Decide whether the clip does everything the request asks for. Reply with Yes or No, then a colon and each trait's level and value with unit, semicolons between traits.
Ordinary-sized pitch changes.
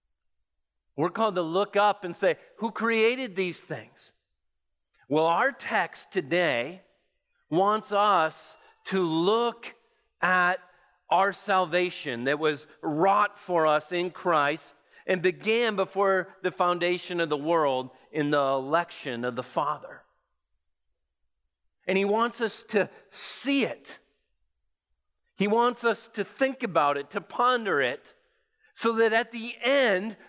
No: wide, 7.2 semitones